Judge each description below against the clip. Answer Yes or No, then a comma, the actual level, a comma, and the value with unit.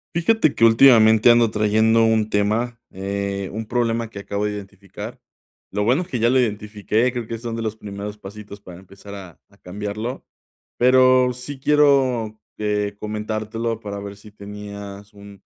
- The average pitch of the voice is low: Yes, low, 110 Hz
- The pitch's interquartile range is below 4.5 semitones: Yes, narrow, 2.6 semitones